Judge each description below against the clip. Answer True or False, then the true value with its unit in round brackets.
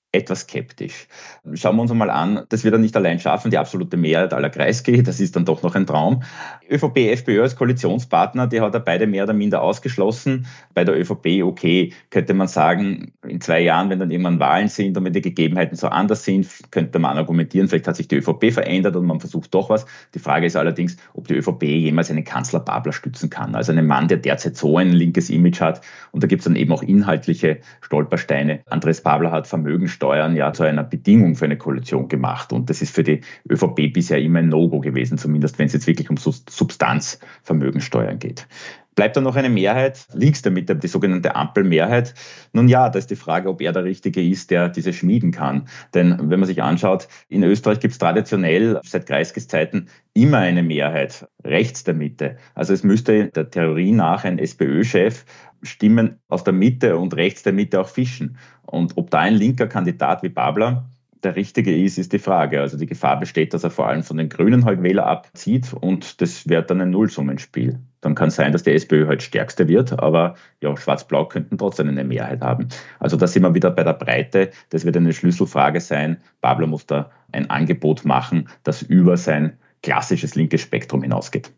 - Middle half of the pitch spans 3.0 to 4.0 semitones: False (4.8 semitones)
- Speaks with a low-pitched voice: True (85 Hz)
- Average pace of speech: False (205 wpm)